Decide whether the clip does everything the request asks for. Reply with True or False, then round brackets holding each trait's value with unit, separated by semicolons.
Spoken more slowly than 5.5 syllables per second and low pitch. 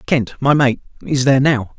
True (5.2 syllables/s; 130 Hz)